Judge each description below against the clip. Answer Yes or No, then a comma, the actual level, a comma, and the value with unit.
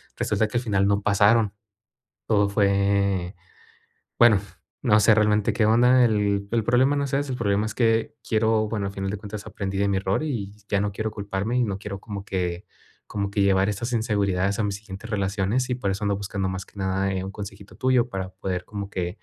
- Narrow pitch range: Yes, narrow, 2.1 semitones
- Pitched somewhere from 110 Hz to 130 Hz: No, low, 100 Hz